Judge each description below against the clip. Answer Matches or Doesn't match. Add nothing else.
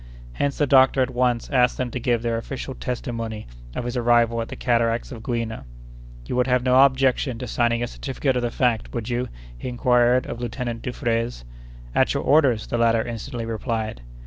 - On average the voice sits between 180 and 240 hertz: Doesn't match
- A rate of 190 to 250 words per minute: Matches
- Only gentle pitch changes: Matches